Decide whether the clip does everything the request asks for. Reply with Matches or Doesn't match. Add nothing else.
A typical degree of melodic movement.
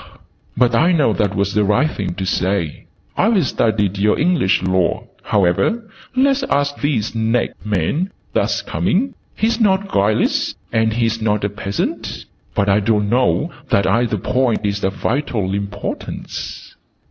Doesn't match